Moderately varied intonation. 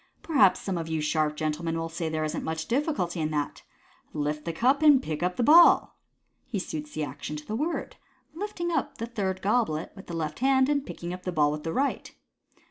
No: wide, 8.9 semitones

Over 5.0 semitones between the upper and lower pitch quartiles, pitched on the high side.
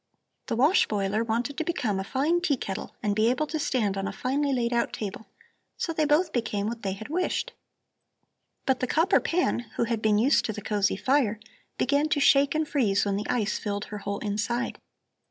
Yes: wide, 5.5 semitones; high, 235 Hz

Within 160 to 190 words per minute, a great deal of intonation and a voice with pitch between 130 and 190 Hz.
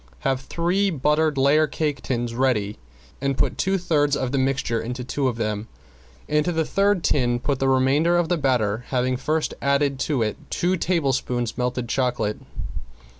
No: average, 170 wpm; average, 3.8 semitones; low, 135 Hz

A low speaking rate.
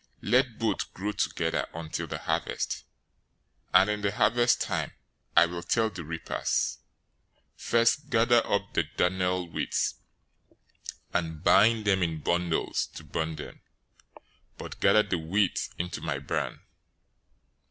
Yes: slow, 130 wpm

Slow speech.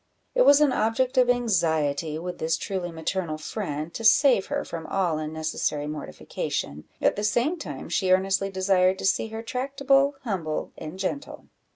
No: average, 165 wpm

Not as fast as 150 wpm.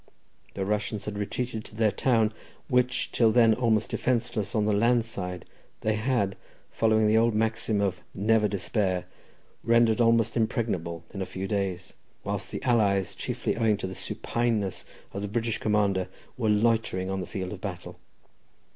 No: average, 165 wpm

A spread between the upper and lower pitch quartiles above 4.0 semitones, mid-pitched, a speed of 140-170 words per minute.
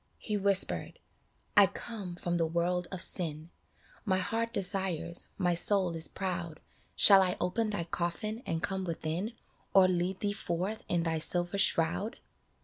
No: average, 2.8 semitones; medium, 180 Hz; average, 155 wpm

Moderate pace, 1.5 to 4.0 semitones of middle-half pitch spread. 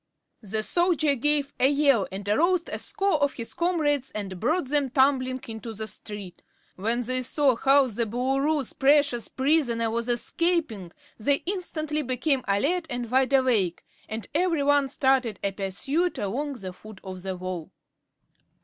No: average, 155 wpm; average, 5.1 semitones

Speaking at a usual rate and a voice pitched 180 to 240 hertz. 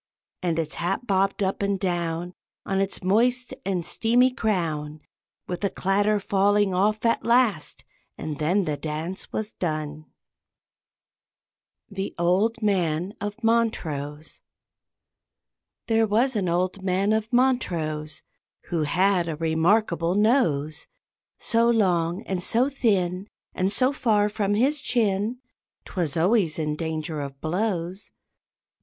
No: slow, 125 wpm; high, 190 Hz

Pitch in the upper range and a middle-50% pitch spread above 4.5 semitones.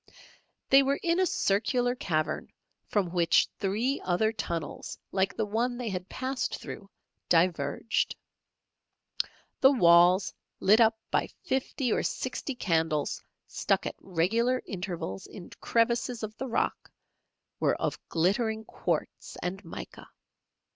Yes: high, 210 Hz; wide, 5.6 semitones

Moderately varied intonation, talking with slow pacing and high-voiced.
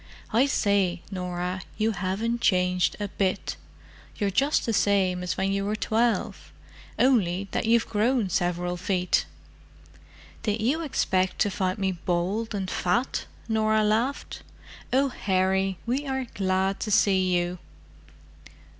Yes: average, 3.5 semitones; slow, 130 wpm; high, 195 Hz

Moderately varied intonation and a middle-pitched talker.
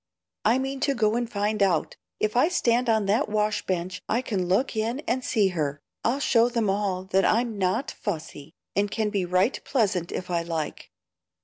No: average, 4.4 semitones; high, 210 Hz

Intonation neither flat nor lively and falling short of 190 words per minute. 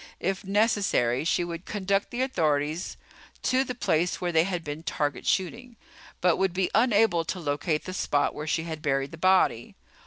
Yes: average, 4.2 semitones; average, 180 wpm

